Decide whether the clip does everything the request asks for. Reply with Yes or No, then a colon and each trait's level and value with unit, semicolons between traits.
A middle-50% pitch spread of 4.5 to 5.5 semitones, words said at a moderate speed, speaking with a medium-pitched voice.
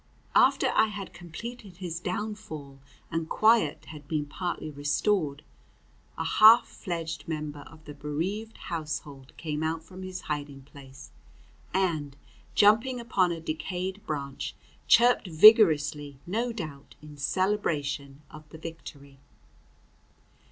No: average, 4.8 semitones; slow, 120 wpm; medium, 160 Hz